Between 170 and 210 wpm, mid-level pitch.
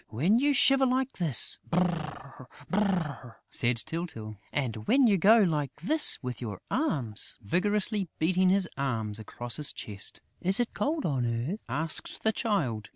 No: average, 155 wpm; medium, 165 Hz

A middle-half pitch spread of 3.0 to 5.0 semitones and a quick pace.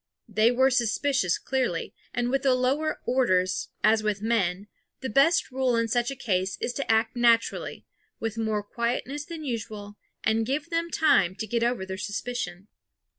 No: average, 3.9 semitones; average, 170 wpm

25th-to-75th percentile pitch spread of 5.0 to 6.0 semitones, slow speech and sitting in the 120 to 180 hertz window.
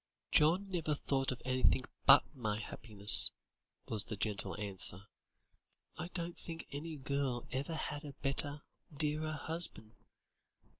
Yes: wide, 5.4 semitones; slow, 130 wpm; medium, 140 Hz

